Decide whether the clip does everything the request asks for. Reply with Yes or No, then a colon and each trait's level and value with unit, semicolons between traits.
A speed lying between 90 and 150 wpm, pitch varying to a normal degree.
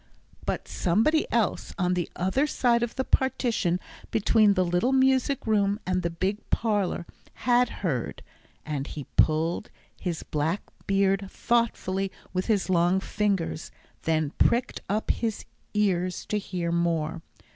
Yes: slow, 135 wpm; average, 4.6 semitones